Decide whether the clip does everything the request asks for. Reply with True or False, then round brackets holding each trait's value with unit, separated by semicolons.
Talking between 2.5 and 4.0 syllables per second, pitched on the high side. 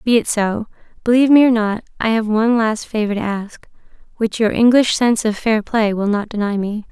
False (5.5 syllables/s; 220 Hz)